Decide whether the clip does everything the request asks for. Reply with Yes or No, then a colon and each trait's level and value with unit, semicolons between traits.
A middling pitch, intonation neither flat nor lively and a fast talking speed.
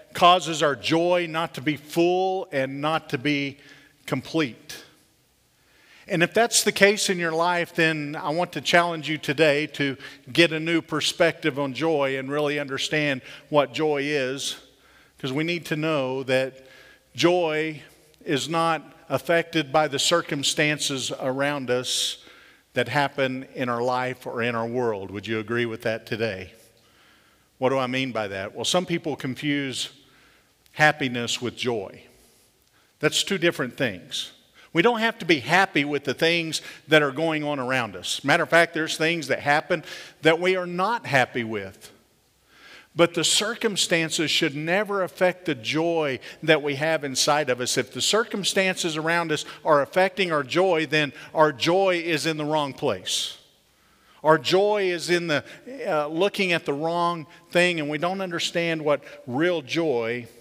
No: medium, 155 Hz; average, 3.8 semitones; average, 165 wpm